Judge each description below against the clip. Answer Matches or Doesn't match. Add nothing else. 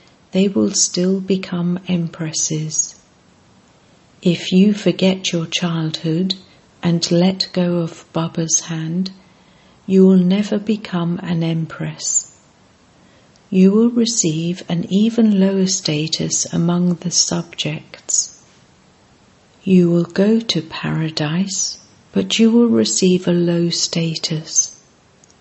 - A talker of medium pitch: Matches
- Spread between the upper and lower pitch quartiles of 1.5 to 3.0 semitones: Matches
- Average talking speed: Doesn't match